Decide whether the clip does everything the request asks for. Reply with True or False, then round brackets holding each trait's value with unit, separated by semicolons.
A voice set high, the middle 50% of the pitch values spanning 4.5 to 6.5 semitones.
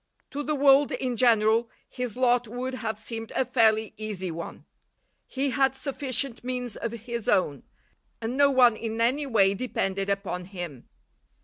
False (235 Hz; 3.3 semitones)